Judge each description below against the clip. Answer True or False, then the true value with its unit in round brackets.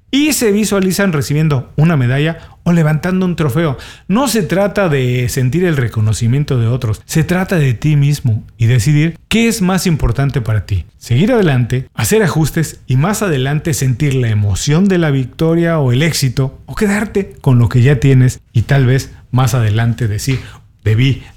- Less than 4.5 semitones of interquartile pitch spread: False (5.4 semitones)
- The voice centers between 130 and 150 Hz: True (140 Hz)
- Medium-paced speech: True (175 wpm)